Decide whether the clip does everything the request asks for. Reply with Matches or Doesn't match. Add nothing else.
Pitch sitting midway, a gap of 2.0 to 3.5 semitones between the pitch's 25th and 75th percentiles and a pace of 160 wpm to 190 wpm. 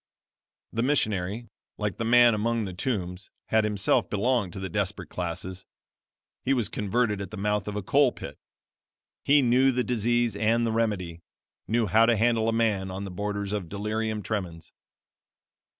Doesn't match